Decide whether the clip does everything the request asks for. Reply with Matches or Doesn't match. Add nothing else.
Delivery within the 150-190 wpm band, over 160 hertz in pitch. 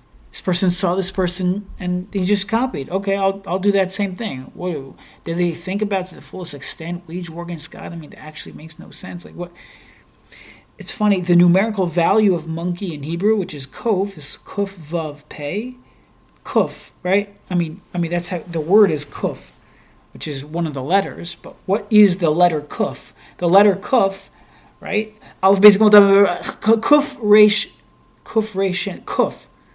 Matches